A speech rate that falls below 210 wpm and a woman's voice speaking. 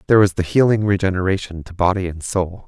No: average, 200 wpm; male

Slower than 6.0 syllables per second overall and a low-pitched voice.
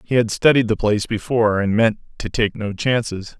Yes: 5.5 syllables/s; low, 110 Hz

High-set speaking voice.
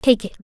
Yes: high, 215 Hz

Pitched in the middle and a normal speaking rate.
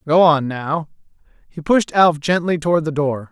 Yes: medium, 160 Hz; average, 180 wpm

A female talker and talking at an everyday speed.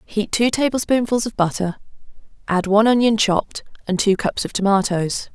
Yes: female; average, 155 wpm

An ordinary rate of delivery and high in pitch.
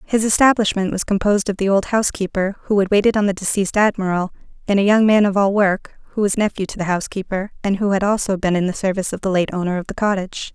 No: fast, 245 wpm; high, 195 Hz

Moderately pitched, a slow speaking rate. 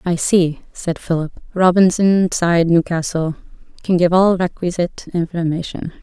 Yes: medium, 175 Hz; slow, 120 wpm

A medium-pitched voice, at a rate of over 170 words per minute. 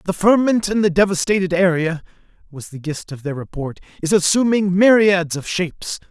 No: medium, 180 Hz; average, 165 wpm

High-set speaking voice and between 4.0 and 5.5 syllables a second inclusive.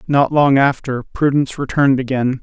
No: low, 135 Hz; 5.2 syllables/s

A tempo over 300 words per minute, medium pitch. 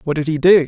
Yes: fast, 355 wpm; medium, 160 Hz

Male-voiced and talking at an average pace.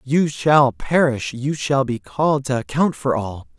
Yes: male; average, 165 wpm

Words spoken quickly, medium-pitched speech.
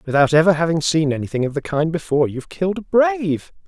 Yes: fast, 210 wpm; medium, 155 Hz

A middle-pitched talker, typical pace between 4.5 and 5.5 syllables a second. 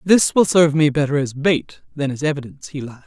No: medium, 145 Hz; 6.3 syllables/s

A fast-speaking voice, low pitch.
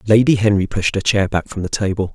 Yes: fast, 250 wpm; low, 100 Hz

